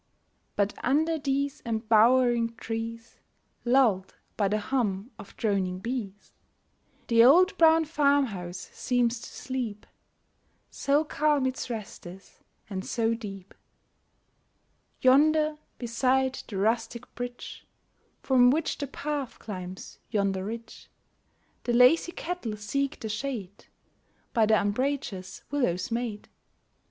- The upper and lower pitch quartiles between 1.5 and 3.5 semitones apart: No, average, 4.6 semitones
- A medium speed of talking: No, slow, 110 wpm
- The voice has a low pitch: No, high, 235 Hz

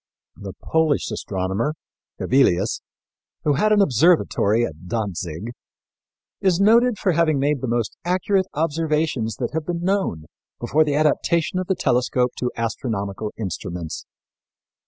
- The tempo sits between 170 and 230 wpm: No, slow, 135 wpm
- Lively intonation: Yes, wide, 7.9 semitones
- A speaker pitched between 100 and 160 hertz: Yes, medium, 140 Hz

